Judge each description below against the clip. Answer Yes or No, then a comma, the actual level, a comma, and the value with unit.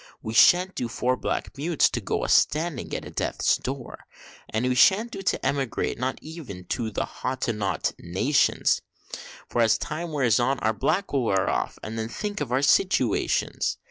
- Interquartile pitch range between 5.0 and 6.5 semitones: Yes, wide, 5.6 semitones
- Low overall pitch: Yes, low, 130 Hz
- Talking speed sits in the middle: Yes, average, 185 wpm